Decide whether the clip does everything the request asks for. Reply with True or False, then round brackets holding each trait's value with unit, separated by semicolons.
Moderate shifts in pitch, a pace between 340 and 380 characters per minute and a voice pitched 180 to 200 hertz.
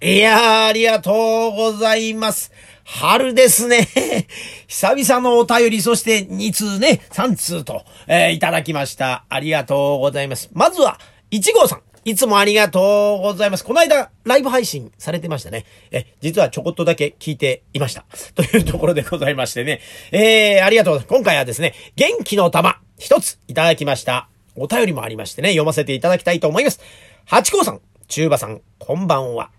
False (7.7 semitones; 370 characters per minute; 185 Hz)